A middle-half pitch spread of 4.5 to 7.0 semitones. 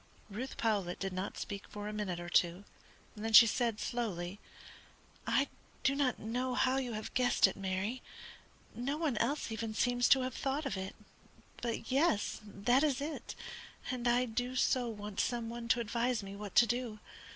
No: average, 3.5 semitones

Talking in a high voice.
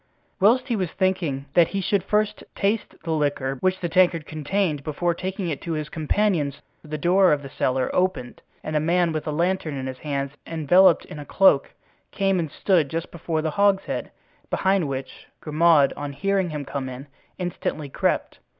No: medium, 165 Hz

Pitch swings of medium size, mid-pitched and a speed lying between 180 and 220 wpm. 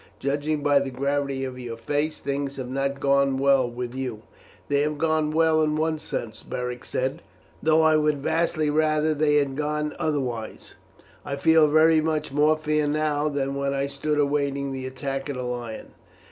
No: narrow, 2.2 semitones; medium, 145 Hz; average, 185 wpm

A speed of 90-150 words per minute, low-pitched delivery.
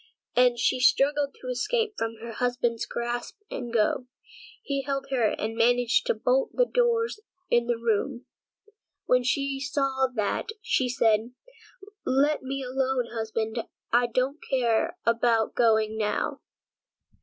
No: average, 145 wpm; very high, 250 Hz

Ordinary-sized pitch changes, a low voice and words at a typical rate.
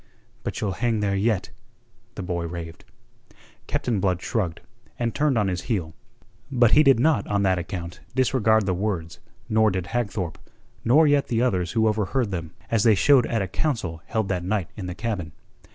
Yes: average, 4.4 semitones; low, 105 Hz; average, 185 wpm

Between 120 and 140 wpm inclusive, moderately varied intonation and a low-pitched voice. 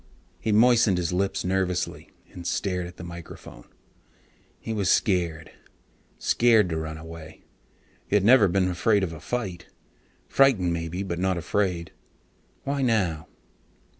Yes: slow, 135 wpm; average, 3.3 semitones; very low, 90 Hz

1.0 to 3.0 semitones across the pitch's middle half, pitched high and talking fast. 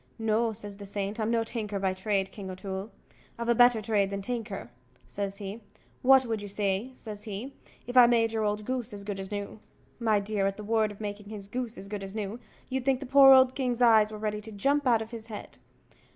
Yes: average, 2.7 semitones; high, 215 Hz; fast, 240 wpm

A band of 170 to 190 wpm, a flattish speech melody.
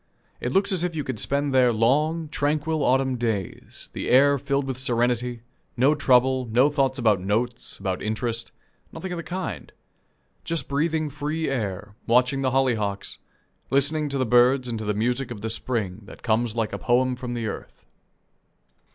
No: average, 175 wpm; average, 3.6 semitones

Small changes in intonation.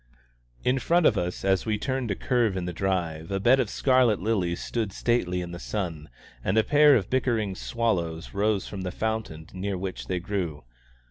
No: average, 4.6 semitones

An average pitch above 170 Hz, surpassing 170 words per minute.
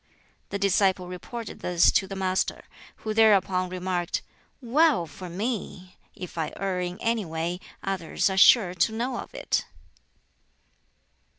No: high, 190 Hz; slow, 135 wpm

